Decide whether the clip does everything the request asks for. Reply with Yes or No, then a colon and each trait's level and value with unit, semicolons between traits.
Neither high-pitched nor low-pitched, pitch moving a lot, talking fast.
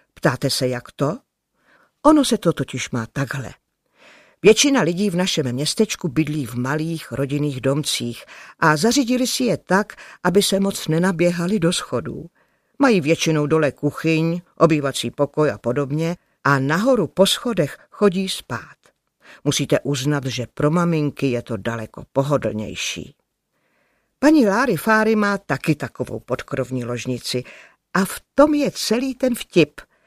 No: medium, 155 Hz; wide, 6.3 semitones; average, 140 wpm